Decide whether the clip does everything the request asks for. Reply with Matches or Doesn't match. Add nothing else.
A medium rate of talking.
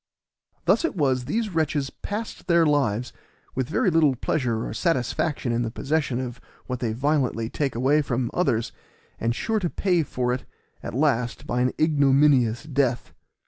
Matches